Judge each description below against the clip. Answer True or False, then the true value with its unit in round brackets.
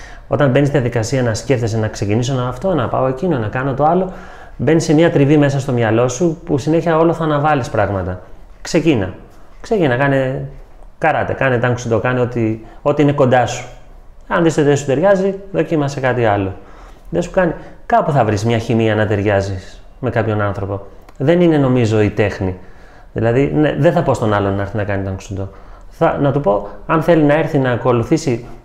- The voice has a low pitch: True (125 Hz)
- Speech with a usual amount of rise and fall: False (5.7 semitones)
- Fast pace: True (190 wpm)